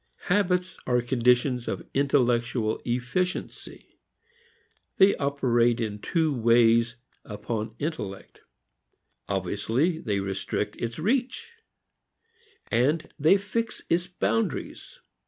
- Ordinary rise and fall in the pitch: No, wide, 6.4 semitones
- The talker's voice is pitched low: Yes, low, 125 Hz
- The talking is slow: Yes, slow, 85 wpm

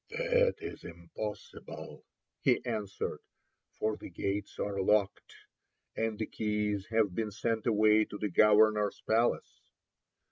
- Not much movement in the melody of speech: Yes, narrow, 1.5 semitones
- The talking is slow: Yes, slow, 120 wpm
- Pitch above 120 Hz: No, low, 105 Hz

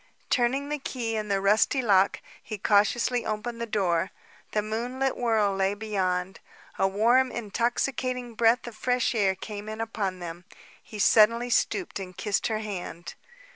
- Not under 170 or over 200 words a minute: No, average, 155 wpm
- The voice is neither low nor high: No, high, 215 Hz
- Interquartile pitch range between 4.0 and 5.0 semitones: No, average, 3.4 semitones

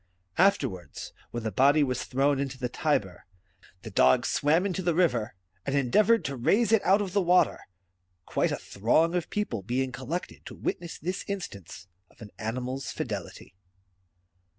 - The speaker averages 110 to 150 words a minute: No, average, 165 wpm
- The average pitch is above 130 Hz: Yes, medium, 140 Hz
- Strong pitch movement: Yes, wide, 7.1 semitones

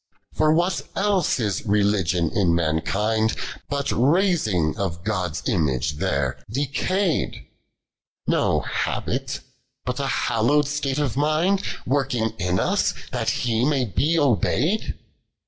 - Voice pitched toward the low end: Yes, low, 120 Hz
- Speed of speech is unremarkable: No, slow, 115 wpm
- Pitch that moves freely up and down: Yes, wide, 7.8 semitones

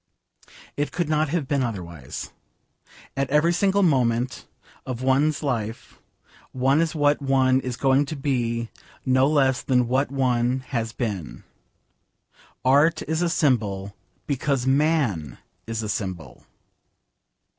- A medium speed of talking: No, slow, 125 wpm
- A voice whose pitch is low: Yes, low, 130 Hz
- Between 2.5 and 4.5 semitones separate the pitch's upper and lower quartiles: Yes, average, 3.9 semitones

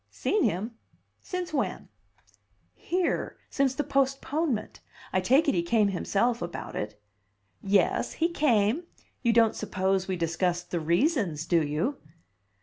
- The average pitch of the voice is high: Yes, high, 215 Hz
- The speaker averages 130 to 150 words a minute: Yes, slow, 135 wpm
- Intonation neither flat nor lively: No, wide, 7.7 semitones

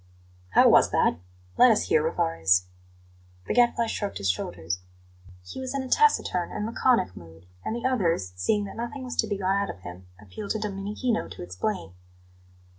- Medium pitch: No, high, 195 Hz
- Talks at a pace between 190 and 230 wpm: No, average, 180 wpm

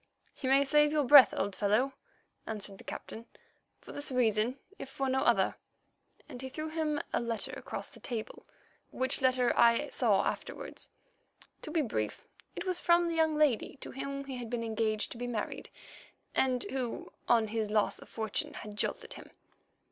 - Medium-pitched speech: No, very high, 250 Hz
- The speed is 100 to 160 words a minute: No, average, 180 wpm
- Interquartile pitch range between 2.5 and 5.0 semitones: Yes, average, 3.9 semitones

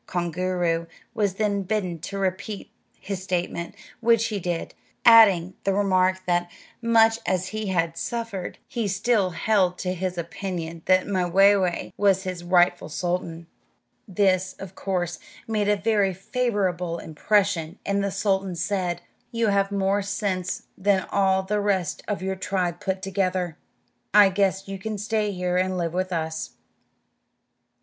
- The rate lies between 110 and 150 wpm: Yes, average, 145 wpm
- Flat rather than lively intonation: Yes, narrow, 2.1 semitones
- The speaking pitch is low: No, high, 190 Hz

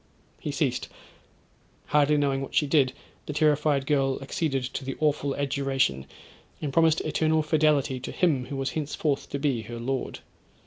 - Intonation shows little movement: Yes, narrow, 2.0 semitones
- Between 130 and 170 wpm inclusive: Yes, average, 150 wpm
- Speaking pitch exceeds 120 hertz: Yes, medium, 140 Hz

